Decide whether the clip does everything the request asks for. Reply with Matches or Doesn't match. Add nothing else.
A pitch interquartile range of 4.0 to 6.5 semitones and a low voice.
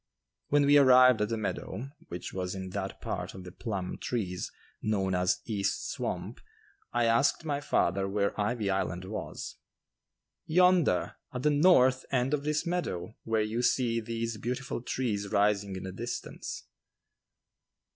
Matches